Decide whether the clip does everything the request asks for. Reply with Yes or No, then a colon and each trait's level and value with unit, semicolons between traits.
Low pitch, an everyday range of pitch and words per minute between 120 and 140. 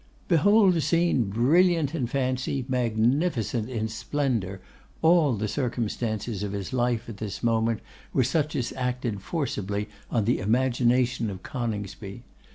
Yes: low, 120 Hz; average, 3.9 semitones; slow, 135 wpm